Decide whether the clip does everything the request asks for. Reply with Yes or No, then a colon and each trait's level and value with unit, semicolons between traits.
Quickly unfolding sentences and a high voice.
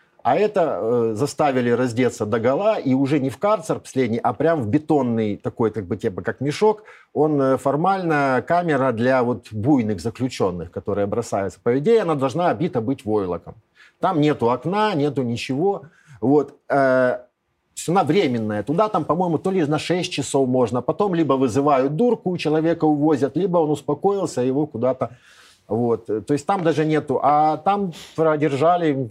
No: fast, 165 wpm; medium, 140 Hz